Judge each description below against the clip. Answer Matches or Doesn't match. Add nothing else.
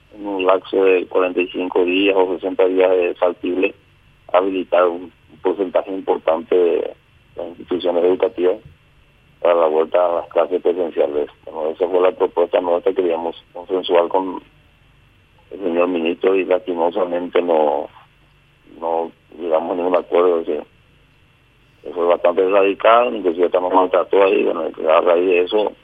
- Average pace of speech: Matches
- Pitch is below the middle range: Matches